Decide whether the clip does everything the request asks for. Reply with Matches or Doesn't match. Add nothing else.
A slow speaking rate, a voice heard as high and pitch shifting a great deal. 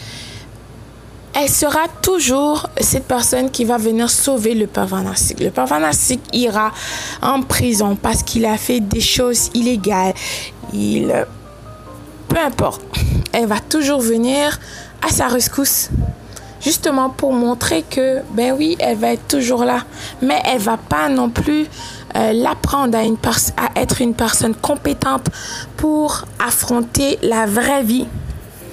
Matches